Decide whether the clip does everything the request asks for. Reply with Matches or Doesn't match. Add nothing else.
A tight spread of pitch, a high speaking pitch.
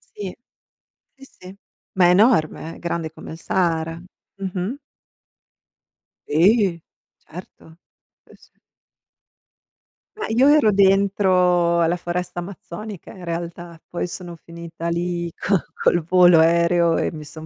Doesn't match